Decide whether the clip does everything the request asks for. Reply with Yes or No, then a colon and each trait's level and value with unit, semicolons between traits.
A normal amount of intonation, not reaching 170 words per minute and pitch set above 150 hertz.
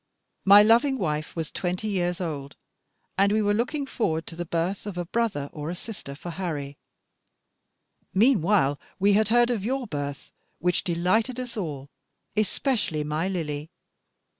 No: wide, 5.8 semitones; average, 150 wpm; medium, 185 Hz